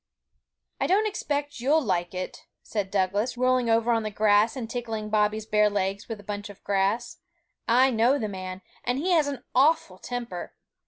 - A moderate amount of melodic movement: Yes, average, 3.9 semitones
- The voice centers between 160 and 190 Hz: No, high, 225 Hz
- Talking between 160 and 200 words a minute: Yes, average, 180 wpm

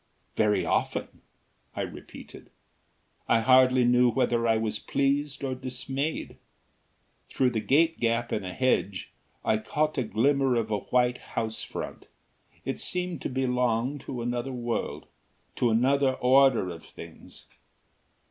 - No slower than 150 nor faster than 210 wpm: No, slow, 135 wpm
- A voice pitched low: Yes, low, 125 Hz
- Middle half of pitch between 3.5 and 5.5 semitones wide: No, average, 2.9 semitones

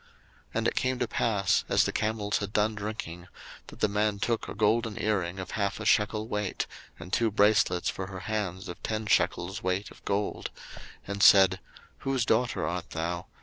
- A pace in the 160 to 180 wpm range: No, average, 190 wpm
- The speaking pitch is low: Yes, low, 105 Hz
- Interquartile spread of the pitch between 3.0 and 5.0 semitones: No, narrow, 2.6 semitones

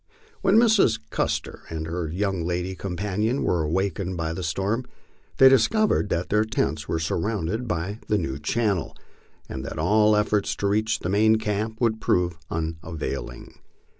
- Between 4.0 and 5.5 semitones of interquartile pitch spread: Yes, average, 4.7 semitones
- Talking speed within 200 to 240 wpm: No, average, 155 wpm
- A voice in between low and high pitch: No, low, 100 Hz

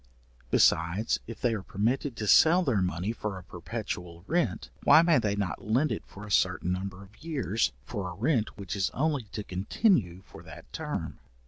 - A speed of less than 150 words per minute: No, average, 190 wpm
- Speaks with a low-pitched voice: Yes, low, 105 Hz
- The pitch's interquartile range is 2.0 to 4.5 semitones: No, average, 5.2 semitones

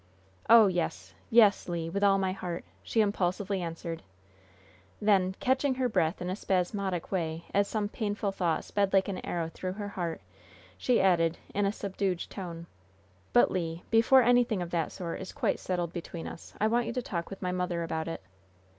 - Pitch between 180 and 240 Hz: Yes, medium, 185 Hz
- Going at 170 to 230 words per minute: Yes, average, 185 wpm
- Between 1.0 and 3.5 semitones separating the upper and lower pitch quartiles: Yes, average, 3.2 semitones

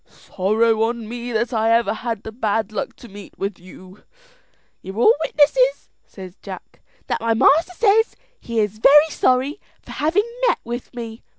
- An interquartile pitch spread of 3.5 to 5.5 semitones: No, average, 2.8 semitones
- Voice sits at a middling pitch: No, high, 230 Hz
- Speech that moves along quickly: No, average, 165 wpm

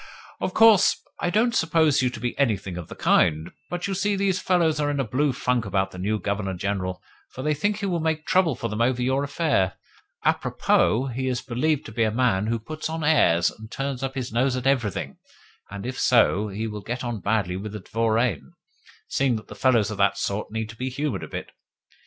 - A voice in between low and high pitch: No, low, 125 Hz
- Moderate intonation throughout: No, wide, 5.8 semitones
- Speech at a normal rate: No, fast, 225 wpm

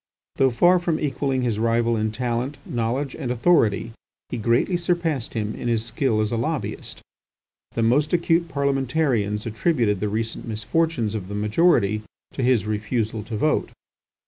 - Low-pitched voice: Yes, low, 120 Hz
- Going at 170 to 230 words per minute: No, average, 155 wpm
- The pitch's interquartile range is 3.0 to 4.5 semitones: No, average, 5.1 semitones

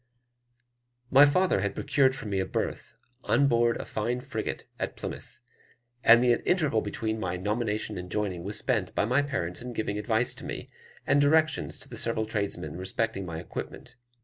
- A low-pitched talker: Yes, low, 110 Hz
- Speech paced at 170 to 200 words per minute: Yes, average, 175 wpm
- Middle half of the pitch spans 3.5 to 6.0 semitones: Yes, average, 3.8 semitones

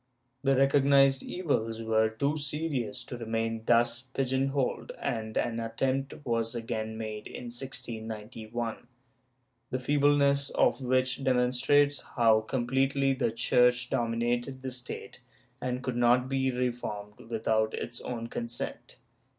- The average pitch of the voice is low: Yes, low, 125 Hz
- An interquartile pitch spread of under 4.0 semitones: Yes, average, 2.8 semitones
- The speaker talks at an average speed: No, slow, 125 wpm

